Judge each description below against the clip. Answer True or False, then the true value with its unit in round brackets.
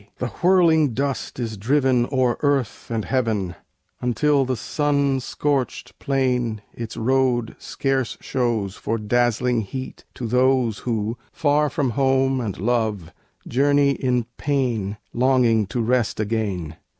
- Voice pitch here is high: False (125 Hz)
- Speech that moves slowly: True (125 wpm)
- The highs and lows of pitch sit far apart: False (3.2 semitones)